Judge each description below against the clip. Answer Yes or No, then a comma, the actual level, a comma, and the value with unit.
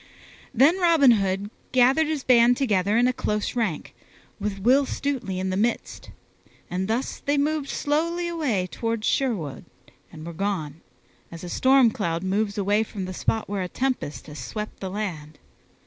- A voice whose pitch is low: No, high, 215 Hz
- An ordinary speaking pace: Yes, average, 165 wpm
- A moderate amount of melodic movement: No, wide, 6.0 semitones